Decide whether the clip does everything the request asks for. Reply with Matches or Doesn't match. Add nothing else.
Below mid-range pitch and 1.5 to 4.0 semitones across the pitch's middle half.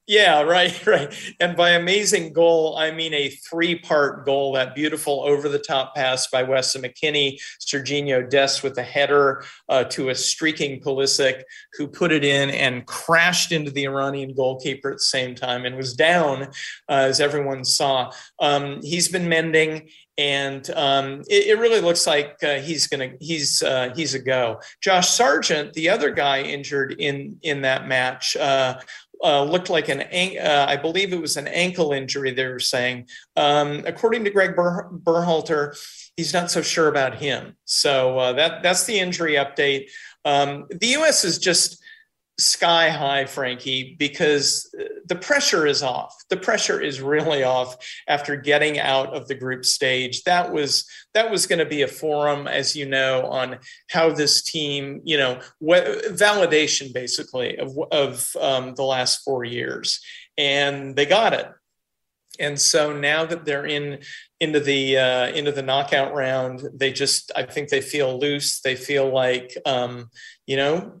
Doesn't match